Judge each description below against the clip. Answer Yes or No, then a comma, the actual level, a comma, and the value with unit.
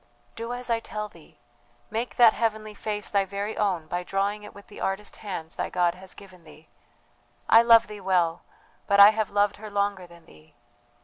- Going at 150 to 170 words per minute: No, average, 195 wpm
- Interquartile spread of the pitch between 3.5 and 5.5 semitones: No, average, 2.8 semitones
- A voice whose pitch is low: No, high, 200 Hz